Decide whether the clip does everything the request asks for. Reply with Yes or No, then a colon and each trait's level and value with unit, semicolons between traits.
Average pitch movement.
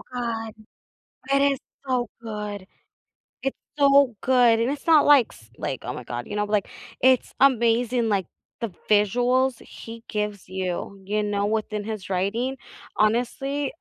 Yes: average, 3.7 semitones